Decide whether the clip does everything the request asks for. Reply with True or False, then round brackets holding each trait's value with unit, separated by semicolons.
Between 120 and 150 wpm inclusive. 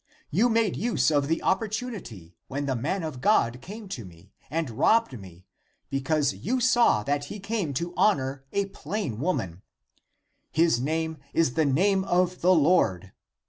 False (165 wpm)